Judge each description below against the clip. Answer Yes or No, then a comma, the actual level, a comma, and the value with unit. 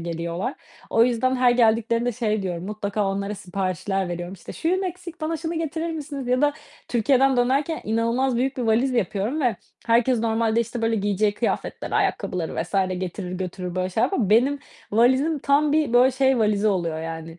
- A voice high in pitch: Yes, high, 230 Hz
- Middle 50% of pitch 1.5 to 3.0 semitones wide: No, average, 5.3 semitones